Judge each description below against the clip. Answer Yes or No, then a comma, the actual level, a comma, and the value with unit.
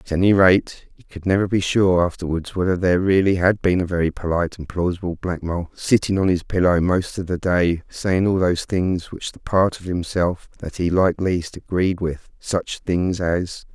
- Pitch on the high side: No, very low, 90 Hz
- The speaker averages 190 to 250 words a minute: Yes, fast, 205 wpm